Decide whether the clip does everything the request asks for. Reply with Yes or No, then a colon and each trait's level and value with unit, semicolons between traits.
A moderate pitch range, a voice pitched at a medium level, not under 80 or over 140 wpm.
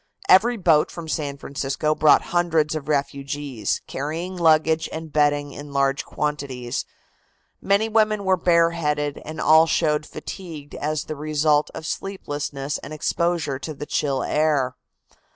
No: narrow, 2.3 semitones; medium, 150 Hz; slow, 135 wpm